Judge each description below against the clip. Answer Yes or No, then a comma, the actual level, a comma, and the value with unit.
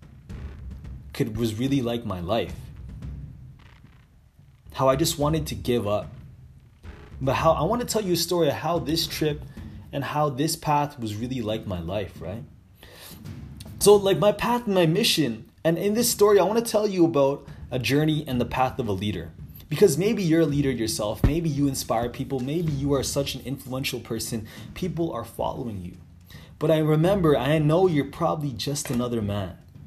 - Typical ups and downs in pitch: No, wide, 6.2 semitones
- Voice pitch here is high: No, medium, 140 Hz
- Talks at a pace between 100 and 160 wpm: No, average, 185 wpm